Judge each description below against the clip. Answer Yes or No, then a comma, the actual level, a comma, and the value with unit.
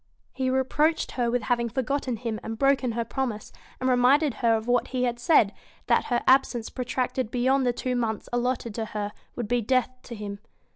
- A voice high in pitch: Yes, high, 245 Hz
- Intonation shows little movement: Yes, narrow, 2.2 semitones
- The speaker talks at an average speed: Yes, average, 195 wpm